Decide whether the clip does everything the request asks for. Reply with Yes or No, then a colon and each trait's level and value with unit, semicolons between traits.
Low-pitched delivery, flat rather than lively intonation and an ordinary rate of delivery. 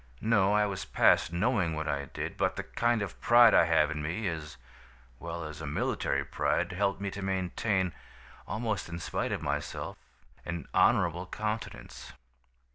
No: very low, 90 Hz; average, 4.2 semitones; average, 165 wpm